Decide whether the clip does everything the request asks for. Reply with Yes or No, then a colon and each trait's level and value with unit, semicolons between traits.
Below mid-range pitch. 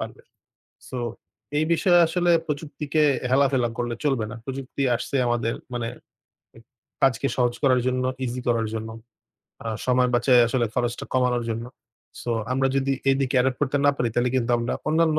Yes: low, 125 Hz